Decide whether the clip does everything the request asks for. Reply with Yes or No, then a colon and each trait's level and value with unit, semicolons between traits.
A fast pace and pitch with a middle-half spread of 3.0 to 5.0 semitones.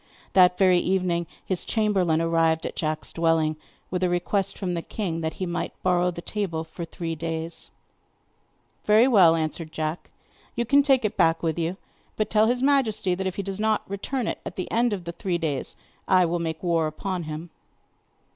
No: average, 195 wpm; average, 3.4 semitones